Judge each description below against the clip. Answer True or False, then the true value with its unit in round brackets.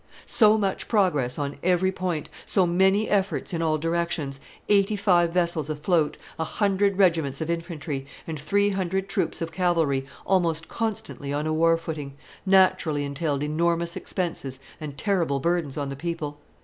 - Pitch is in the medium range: True (170 Hz)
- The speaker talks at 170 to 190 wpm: False (155 wpm)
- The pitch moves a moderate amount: True (4.1 semitones)